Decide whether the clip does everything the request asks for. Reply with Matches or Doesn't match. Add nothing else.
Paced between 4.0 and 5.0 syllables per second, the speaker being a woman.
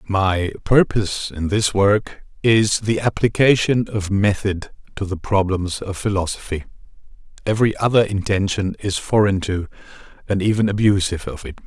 Doesn't match